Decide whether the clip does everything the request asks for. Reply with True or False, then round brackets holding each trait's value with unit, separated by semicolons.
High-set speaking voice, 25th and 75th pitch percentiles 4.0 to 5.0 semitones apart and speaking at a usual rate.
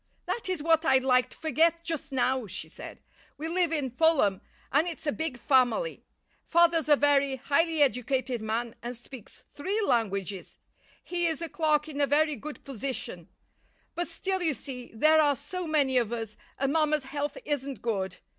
True (285 Hz; 4.3 semitones; 175 wpm)